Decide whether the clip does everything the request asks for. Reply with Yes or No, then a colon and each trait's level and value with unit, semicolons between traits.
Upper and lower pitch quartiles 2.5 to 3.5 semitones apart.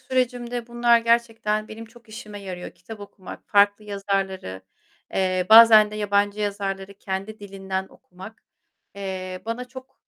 Yes: average, 2.9 semitones